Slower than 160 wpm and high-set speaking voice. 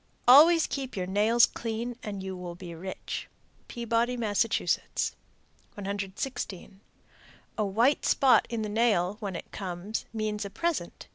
Yes: slow, 135 wpm; high, 215 Hz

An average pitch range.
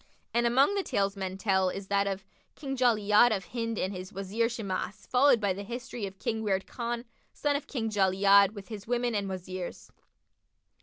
Yes: average, 3.5 semitones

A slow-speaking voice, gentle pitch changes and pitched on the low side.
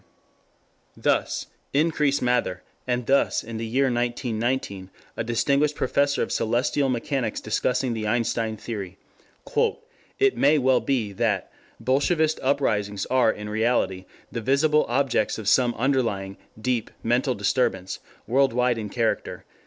No: slow, 130 wpm; average, 3.7 semitones; low, 120 Hz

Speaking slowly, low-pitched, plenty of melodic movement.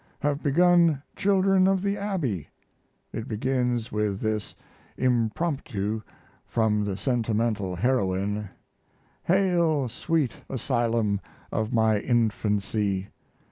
Yes: slow, 95 wpm; low, 115 Hz; wide, 5.9 semitones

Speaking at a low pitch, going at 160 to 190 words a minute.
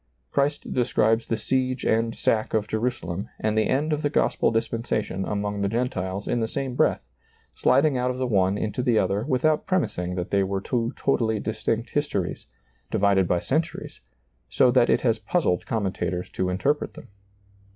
Yes: low, 115 Hz; average, 175 wpm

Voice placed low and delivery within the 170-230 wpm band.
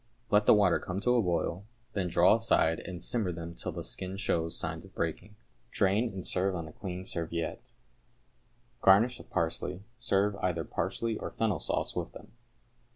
Yes: very low, 95 Hz; average, 175 wpm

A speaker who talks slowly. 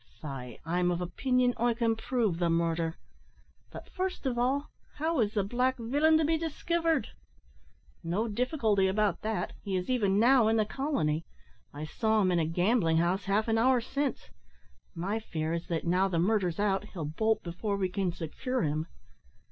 No: average, 180 wpm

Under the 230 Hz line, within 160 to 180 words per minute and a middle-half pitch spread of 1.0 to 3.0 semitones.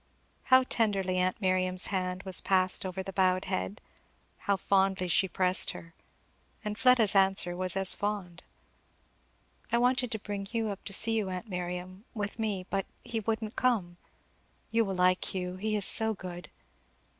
Yes: high, 190 Hz; average, 165 wpm; narrow, 2.6 semitones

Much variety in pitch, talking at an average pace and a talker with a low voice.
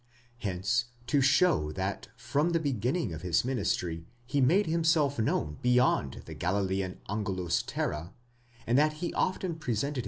Yes: wide, 8.0 semitones; average, 145 wpm; low, 120 Hz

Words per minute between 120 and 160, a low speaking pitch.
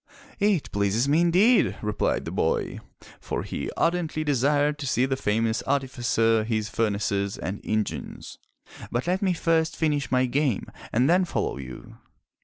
Yes: average, 155 wpm; low, 130 Hz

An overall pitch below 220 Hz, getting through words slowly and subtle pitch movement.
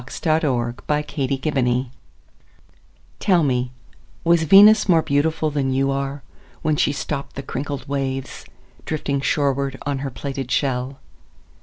Yes: medium, 140 Hz; slow, 105 wpm; narrow, 2.1 semitones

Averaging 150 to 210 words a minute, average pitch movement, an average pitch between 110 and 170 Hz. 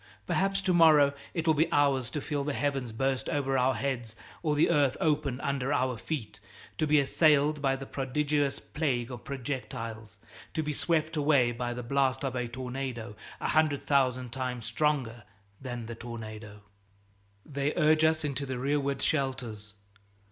Yes: average, 165 wpm; average, 3.2 semitones; low, 135 Hz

